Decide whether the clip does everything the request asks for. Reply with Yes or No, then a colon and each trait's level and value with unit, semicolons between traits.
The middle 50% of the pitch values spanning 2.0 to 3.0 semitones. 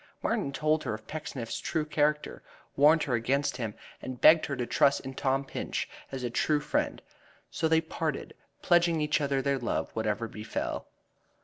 No: average, 3.5 semitones